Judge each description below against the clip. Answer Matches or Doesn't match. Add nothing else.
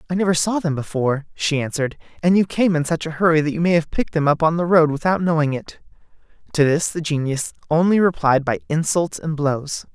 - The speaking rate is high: Matches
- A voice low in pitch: Doesn't match